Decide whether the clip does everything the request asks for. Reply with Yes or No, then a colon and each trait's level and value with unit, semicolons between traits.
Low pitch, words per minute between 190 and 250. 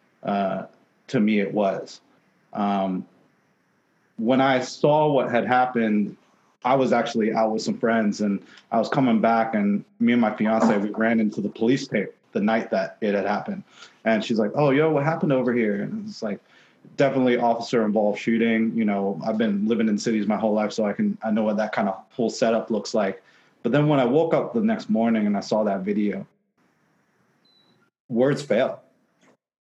Yes: low, 115 Hz; average, 195 wpm